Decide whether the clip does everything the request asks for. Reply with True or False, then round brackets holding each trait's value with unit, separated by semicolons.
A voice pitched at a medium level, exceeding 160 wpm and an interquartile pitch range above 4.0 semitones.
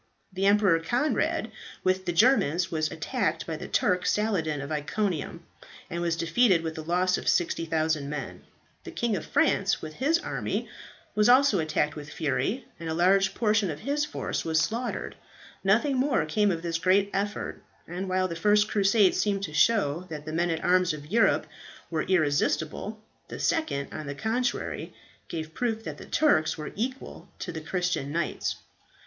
True (180 Hz; 175 wpm; 4.9 semitones)